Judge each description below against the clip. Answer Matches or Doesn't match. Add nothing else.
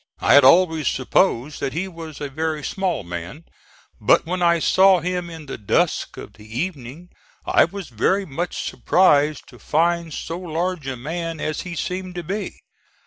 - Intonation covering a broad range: Doesn't match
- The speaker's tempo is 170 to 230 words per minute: Matches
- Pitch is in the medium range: Matches